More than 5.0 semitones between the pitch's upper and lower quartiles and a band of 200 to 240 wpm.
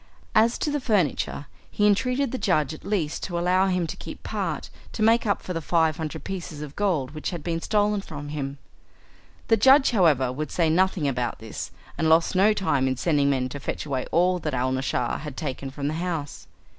Yes: wide, 5.4 semitones; fast, 205 wpm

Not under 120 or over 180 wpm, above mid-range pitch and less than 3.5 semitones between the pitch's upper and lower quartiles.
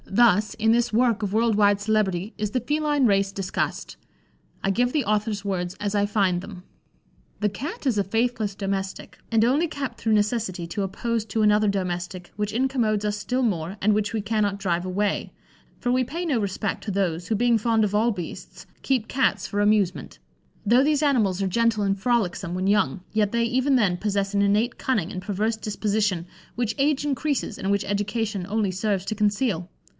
No: average, 190 wpm; high, 210 Hz; average, 3.0 semitones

